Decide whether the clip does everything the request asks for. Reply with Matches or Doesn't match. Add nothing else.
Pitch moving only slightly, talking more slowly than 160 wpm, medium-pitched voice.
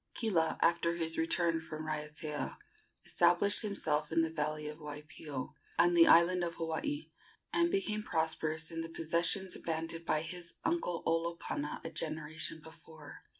Matches